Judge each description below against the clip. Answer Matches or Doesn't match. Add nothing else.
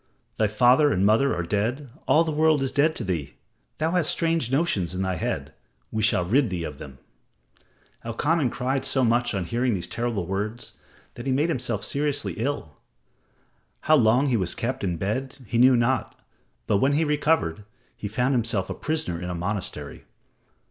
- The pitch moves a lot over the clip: Matches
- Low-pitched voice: Matches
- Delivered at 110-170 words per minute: Doesn't match